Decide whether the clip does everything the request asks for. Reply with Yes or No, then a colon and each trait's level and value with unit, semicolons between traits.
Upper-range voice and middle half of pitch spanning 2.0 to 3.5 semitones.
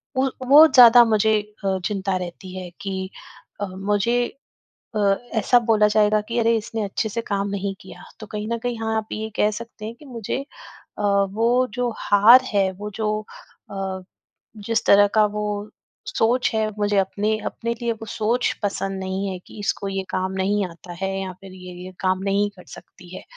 Yes: high, 210 Hz; average, 2.8 semitones